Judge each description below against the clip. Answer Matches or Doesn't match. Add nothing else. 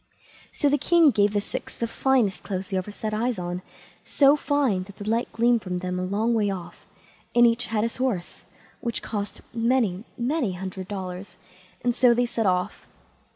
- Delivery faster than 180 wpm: Matches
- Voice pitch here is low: Doesn't match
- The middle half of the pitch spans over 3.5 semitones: Matches